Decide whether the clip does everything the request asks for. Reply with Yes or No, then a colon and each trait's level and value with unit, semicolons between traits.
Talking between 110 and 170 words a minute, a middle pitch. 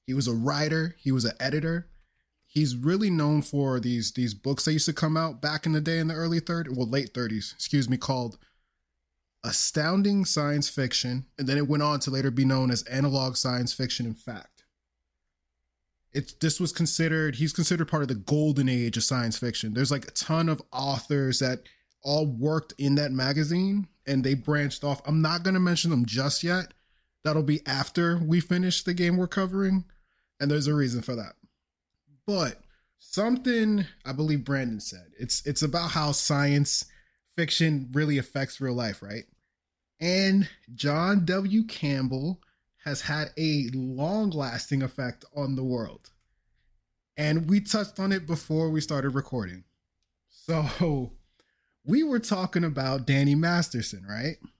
Yes: average, 165 wpm; medium, 145 Hz